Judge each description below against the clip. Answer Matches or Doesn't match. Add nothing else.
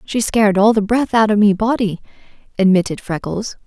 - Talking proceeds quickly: Doesn't match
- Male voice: Doesn't match